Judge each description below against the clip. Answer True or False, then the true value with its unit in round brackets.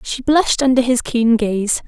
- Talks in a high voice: True (245 Hz)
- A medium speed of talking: True (190 wpm)